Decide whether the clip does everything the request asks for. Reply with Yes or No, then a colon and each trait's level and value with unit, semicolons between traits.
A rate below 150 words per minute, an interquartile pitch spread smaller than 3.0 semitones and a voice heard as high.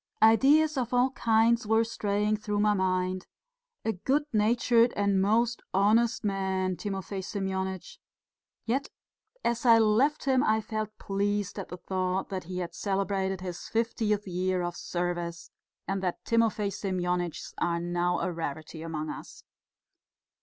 No: average, 140 wpm; average, 3.4 semitones; high, 200 Hz